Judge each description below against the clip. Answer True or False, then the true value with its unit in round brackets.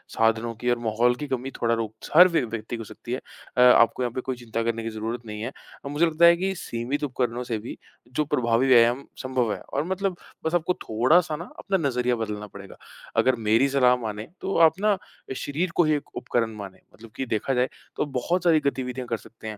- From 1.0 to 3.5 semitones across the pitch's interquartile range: False (4.3 semitones)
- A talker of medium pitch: False (125 Hz)